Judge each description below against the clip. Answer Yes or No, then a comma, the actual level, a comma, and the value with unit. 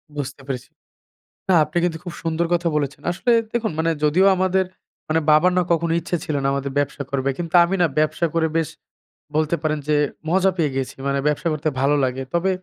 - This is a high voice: No, medium, 160 Hz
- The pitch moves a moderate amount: Yes, average, 3.3 semitones